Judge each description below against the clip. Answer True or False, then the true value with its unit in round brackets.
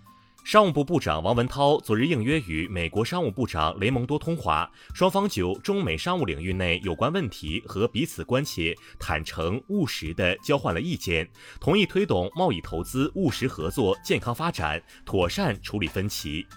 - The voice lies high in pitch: False (115 Hz)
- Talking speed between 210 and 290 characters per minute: True (270 characters per minute)